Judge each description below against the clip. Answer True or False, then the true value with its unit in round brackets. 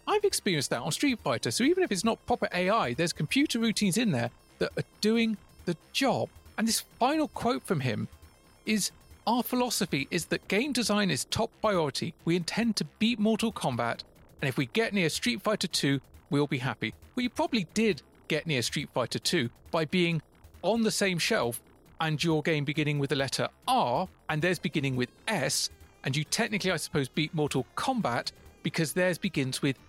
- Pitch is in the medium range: True (180 Hz)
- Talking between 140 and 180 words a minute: False (195 wpm)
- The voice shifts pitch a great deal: True (7.4 semitones)